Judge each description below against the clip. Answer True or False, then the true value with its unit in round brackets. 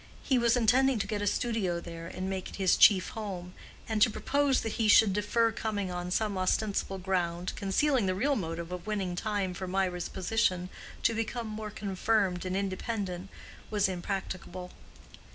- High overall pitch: True (195 Hz)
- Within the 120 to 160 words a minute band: False (170 wpm)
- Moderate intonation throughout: True (3.2 semitones)